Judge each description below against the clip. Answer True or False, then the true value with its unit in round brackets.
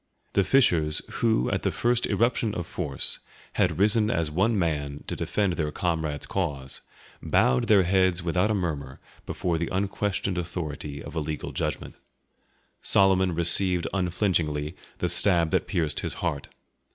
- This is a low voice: True (85 Hz)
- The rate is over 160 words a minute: False (150 wpm)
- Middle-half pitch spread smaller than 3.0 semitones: False (4.2 semitones)